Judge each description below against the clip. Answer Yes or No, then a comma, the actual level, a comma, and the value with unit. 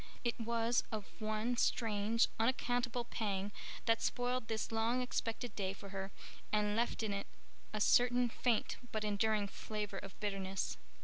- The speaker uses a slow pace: No, average, 145 wpm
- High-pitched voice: Yes, high, 220 Hz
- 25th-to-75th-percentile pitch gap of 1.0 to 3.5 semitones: Yes, narrow, 2.6 semitones